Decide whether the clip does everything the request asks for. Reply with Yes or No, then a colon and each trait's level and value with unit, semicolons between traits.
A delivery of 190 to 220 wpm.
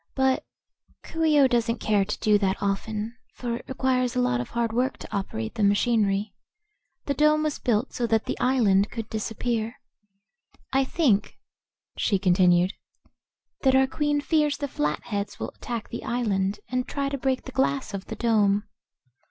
No: average, 170 wpm